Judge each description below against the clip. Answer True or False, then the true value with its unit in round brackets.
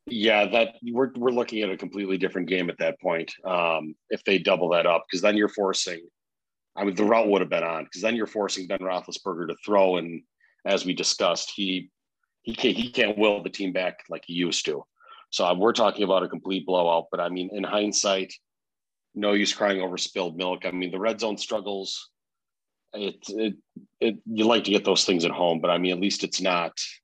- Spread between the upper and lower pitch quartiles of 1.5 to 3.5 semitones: True (2.8 semitones)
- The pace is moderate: False (220 wpm)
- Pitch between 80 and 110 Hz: True (100 Hz)